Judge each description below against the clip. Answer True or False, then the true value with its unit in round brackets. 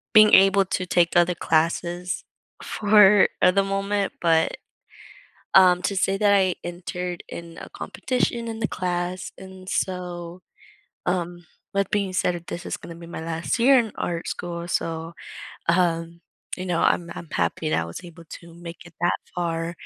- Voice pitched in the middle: True (175 Hz)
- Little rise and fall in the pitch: True (2.1 semitones)